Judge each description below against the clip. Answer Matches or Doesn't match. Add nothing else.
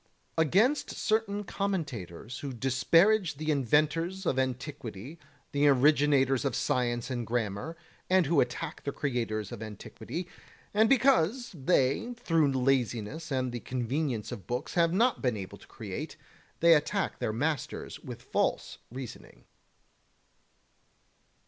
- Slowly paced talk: Matches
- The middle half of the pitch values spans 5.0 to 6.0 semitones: Matches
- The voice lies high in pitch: Doesn't match